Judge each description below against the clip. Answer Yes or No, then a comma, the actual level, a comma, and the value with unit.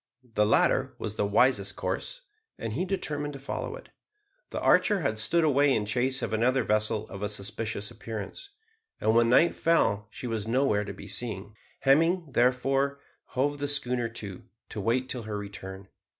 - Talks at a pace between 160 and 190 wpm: Yes, average, 175 wpm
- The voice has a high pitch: No, low, 115 Hz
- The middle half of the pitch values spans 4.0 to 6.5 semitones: Yes, average, 4.6 semitones